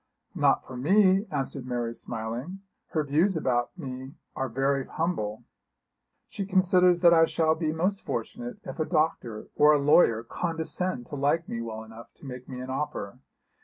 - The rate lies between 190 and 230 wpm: No, average, 165 wpm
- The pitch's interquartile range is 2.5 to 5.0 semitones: No, wide, 5.6 semitones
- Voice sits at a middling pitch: Yes, medium, 145 Hz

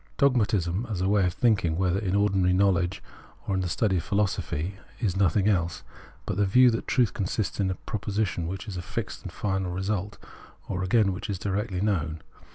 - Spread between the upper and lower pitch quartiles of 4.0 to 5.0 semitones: No, narrow, 2.5 semitones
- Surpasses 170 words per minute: Yes, average, 195 wpm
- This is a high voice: No, very low, 95 Hz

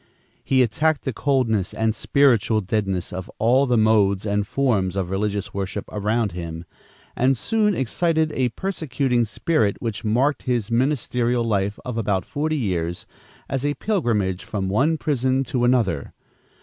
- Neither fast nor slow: Yes, average, 150 wpm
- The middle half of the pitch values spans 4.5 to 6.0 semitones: Yes, average, 5.0 semitones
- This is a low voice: Yes, low, 115 Hz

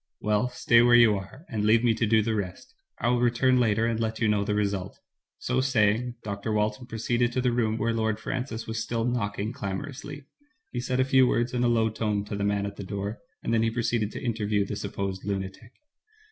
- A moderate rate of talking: No, fast, 225 wpm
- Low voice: Yes, low, 110 Hz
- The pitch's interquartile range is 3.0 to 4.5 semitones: No, narrow, 2.6 semitones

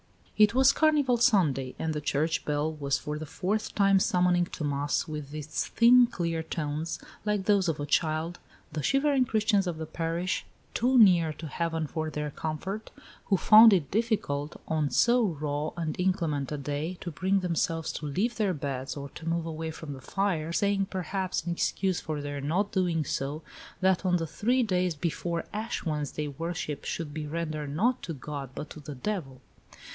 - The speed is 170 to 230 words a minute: Yes, average, 185 wpm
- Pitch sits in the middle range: Yes, medium, 165 Hz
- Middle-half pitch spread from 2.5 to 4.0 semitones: No, average, 4.5 semitones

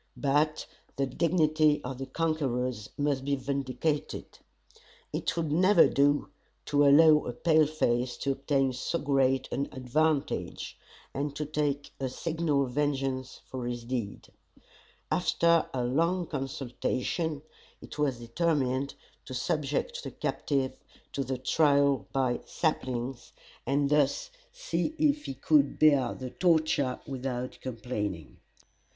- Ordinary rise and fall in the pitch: Yes, average, 3.0 semitones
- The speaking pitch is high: No, medium, 140 Hz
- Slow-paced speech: Yes, slow, 125 wpm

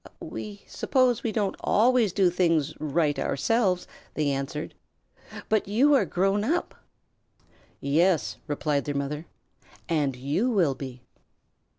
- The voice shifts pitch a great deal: Yes, wide, 6.7 semitones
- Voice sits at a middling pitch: Yes, medium, 175 Hz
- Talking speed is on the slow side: Yes, slow, 120 wpm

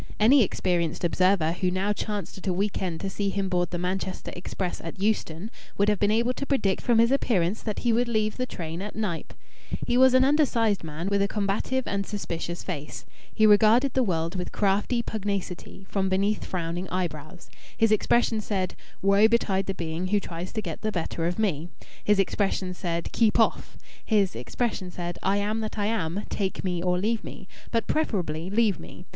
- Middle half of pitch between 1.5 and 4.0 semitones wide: Yes, average, 3.3 semitones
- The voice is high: Yes, high, 195 Hz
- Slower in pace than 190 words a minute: No, average, 195 wpm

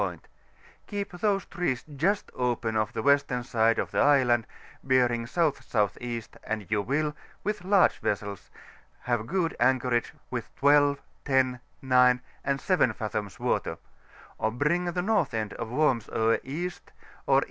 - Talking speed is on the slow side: No, average, 145 wpm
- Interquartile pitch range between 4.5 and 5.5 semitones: Yes, average, 5.1 semitones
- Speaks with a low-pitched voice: Yes, low, 130 Hz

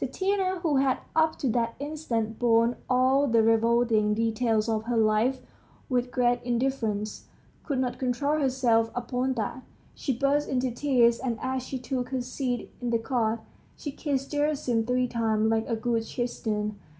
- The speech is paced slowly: No, average, 160 wpm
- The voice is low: No, high, 245 Hz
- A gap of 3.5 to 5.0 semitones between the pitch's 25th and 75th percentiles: No, average, 2.8 semitones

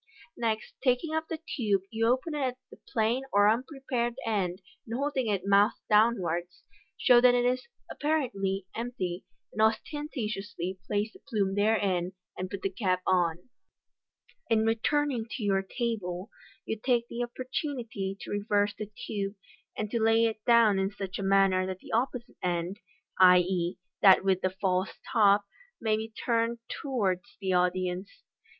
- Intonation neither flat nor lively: Yes, average, 3.9 semitones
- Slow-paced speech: No, average, 155 wpm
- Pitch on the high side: Yes, high, 215 Hz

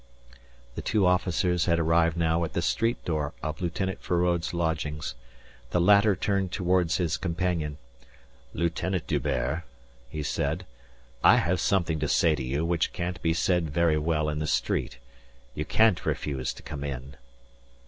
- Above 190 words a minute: No, average, 155 wpm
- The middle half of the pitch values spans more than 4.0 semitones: No, average, 2.8 semitones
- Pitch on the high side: No, very low, 85 Hz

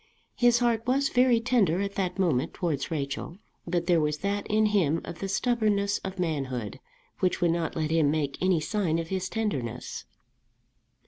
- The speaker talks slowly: No, average, 175 wpm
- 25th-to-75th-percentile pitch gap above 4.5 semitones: Yes, average, 5.1 semitones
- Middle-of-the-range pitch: Yes, medium, 180 Hz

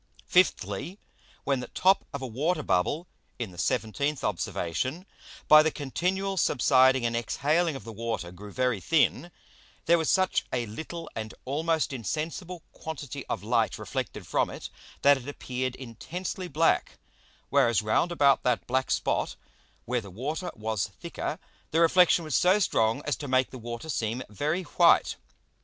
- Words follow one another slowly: No, average, 155 wpm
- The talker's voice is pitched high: No, low, 135 Hz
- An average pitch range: No, wide, 5.8 semitones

